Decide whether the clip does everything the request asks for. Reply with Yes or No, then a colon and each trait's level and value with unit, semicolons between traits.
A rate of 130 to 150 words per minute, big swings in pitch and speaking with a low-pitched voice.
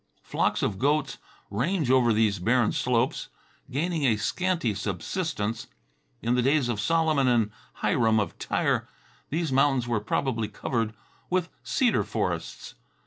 Yes: slow, 135 wpm; wide, 5.7 semitones; low, 125 Hz